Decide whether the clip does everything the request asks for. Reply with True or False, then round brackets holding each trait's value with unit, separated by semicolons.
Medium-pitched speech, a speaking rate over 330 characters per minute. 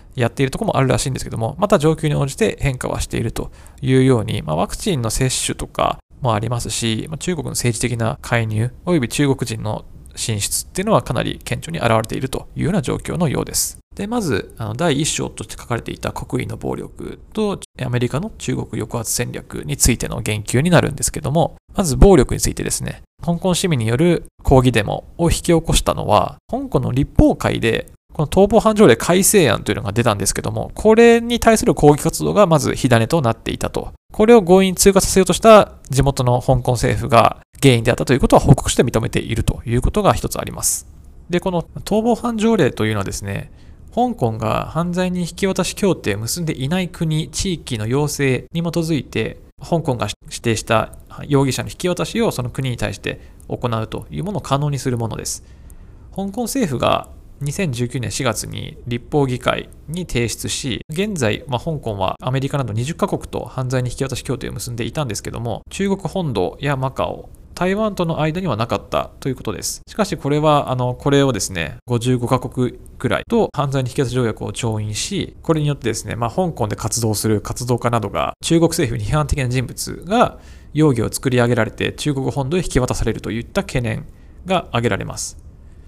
False (130 Hz; 395 characters per minute)